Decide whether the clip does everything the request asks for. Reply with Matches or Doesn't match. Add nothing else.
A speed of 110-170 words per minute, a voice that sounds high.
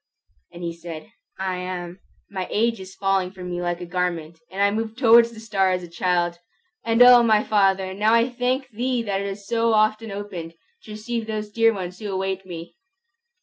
Doesn't match